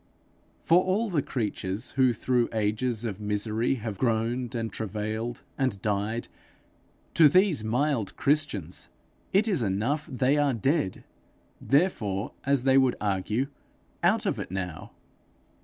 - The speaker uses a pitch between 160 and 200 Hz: No, low, 120 Hz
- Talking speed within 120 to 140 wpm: Yes, slow, 135 wpm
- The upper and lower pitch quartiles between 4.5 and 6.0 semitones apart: Yes, average, 4.8 semitones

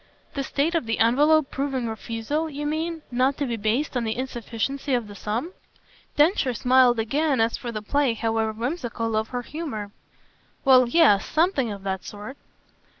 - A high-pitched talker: Yes, very high, 250 Hz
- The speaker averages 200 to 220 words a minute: No, average, 170 wpm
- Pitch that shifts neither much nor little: Yes, average, 4.5 semitones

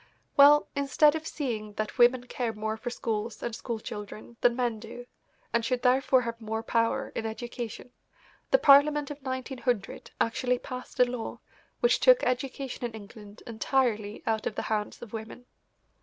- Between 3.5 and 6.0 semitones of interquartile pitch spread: No, average, 2.7 semitones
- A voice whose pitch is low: No, high, 240 Hz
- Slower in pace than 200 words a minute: Yes, average, 165 wpm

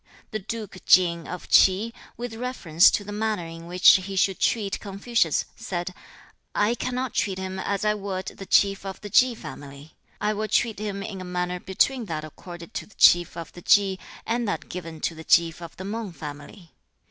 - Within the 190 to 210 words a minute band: Yes, average, 195 wpm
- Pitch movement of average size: Yes, average, 3.5 semitones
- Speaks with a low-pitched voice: No, high, 190 Hz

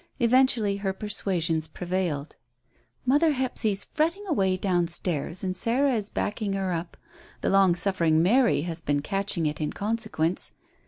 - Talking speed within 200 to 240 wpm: No, average, 145 wpm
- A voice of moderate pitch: No, high, 195 Hz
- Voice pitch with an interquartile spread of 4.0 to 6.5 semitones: Yes, average, 5.0 semitones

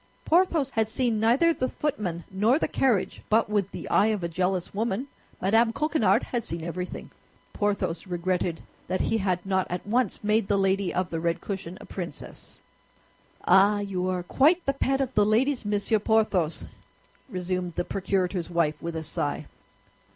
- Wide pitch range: No, average, 3.9 semitones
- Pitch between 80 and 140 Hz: No, high, 200 Hz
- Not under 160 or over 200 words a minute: Yes, average, 170 wpm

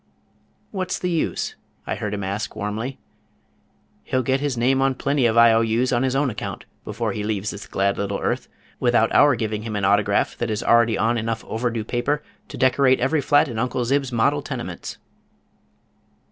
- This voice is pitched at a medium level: No, low, 120 Hz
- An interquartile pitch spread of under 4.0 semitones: Yes, average, 3.6 semitones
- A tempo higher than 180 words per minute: Yes, average, 190 wpm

